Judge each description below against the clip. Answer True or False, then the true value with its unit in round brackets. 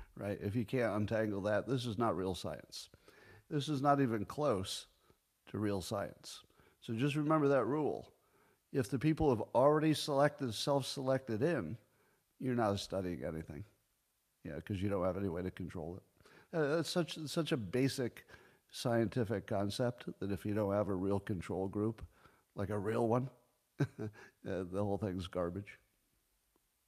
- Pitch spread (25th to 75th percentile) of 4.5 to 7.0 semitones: True (5.1 semitones)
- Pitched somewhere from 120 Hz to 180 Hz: False (110 Hz)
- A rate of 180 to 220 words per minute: False (165 wpm)